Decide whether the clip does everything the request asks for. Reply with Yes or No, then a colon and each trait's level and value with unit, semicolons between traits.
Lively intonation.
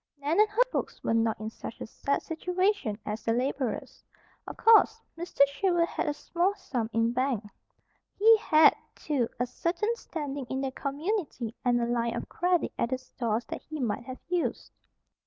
Yes: wide, 6.8 semitones